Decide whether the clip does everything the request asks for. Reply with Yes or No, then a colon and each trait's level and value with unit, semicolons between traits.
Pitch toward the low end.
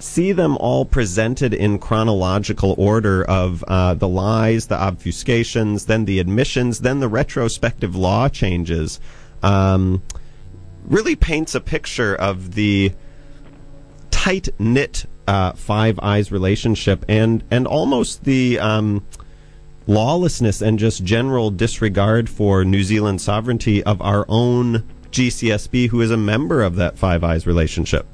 Yes: low, 110 Hz